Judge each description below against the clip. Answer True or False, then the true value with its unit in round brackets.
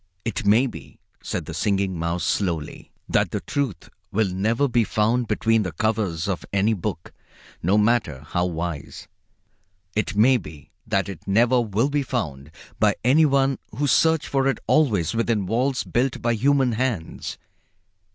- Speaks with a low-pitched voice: True (110 Hz)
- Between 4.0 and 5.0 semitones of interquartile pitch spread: False (5.5 semitones)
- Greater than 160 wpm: False (155 wpm)